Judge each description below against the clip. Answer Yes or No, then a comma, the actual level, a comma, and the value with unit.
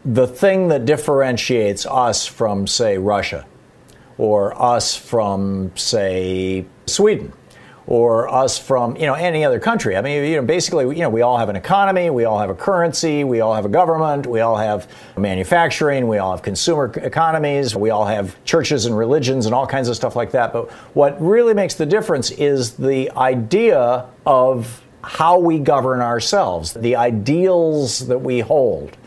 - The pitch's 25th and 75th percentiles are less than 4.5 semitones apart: No, wide, 5.6 semitones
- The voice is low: Yes, low, 125 Hz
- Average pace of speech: Yes, average, 175 wpm